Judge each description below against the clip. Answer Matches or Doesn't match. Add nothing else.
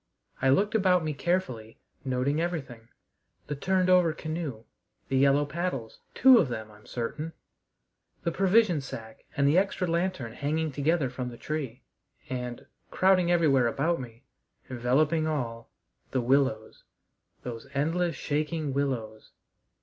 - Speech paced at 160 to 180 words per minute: Doesn't match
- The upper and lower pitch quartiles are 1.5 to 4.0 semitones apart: Doesn't match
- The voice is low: Doesn't match